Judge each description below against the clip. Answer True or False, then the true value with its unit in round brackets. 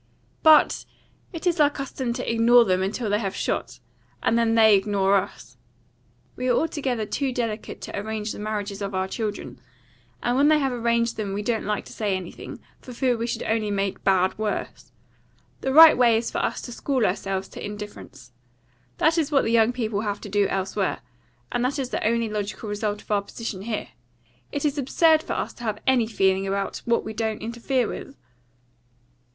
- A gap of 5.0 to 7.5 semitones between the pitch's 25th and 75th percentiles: False (3.4 semitones)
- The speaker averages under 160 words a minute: False (195 wpm)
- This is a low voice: False (220 Hz)